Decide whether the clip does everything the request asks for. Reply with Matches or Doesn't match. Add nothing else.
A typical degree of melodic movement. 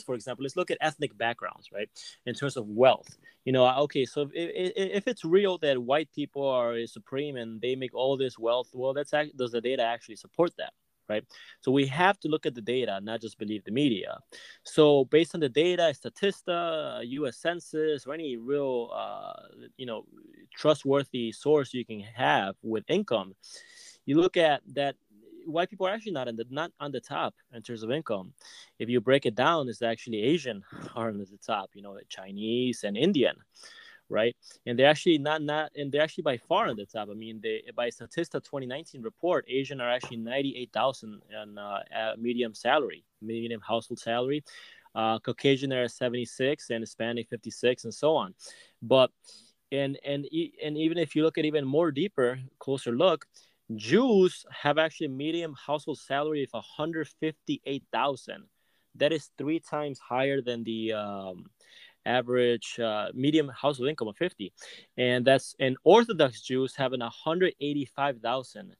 Matches